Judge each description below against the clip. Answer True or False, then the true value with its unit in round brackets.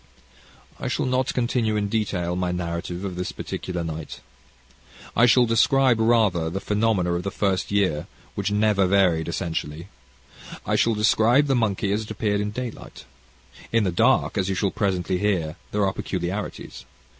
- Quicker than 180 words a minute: False (165 wpm)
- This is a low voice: True (100 Hz)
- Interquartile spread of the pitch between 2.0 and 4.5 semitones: True (3.9 semitones)